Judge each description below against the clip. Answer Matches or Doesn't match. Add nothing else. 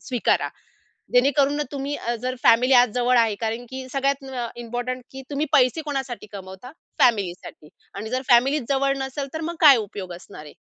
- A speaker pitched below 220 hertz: Doesn't match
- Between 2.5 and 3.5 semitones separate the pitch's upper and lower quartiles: Matches